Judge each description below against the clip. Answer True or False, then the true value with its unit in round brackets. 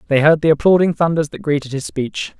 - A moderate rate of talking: False (225 wpm)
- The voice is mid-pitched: True (155 Hz)